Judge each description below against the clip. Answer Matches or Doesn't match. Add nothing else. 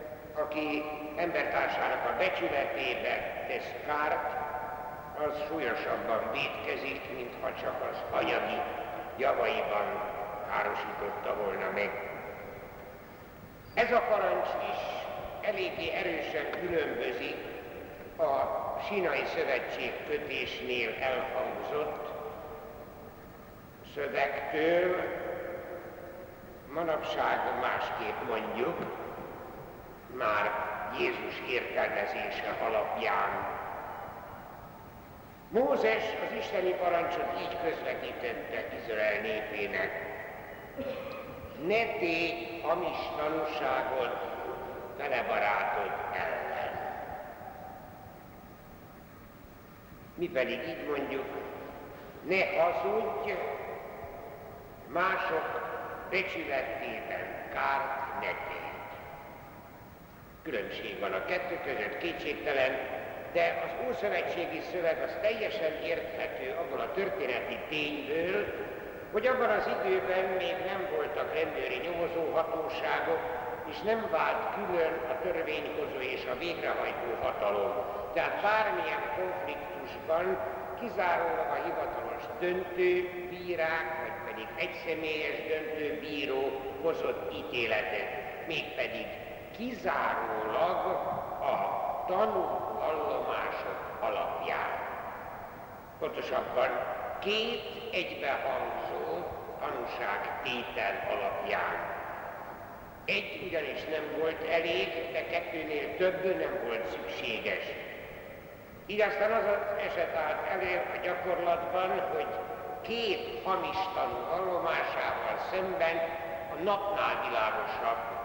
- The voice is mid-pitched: Matches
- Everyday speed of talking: Doesn't match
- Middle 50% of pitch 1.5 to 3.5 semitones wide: Doesn't match